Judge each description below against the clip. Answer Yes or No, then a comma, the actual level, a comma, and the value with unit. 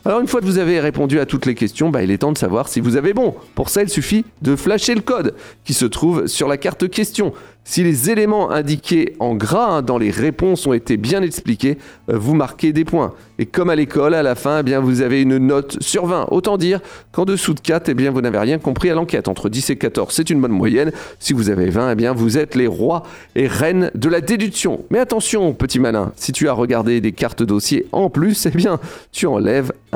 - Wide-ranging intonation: Yes, wide, 6.2 semitones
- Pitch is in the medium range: Yes, medium, 150 Hz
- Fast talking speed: Yes, fast, 250 wpm